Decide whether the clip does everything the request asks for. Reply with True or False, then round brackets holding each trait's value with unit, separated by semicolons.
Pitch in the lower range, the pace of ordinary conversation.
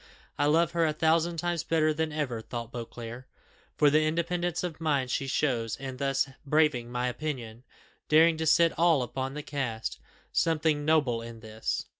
False (150 Hz; 170 wpm)